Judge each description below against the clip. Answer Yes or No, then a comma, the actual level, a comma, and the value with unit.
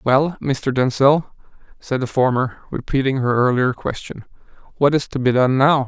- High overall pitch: No, low, 135 Hz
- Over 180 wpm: No, average, 165 wpm